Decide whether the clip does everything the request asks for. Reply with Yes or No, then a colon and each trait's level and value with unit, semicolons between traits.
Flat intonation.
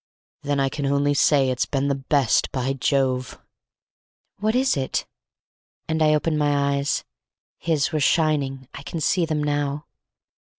Yes: narrow, 2.0 semitones